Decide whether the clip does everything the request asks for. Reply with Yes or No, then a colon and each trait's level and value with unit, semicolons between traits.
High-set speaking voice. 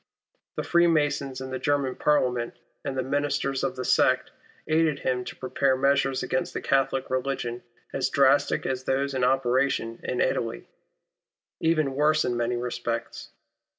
No: low, 135 Hz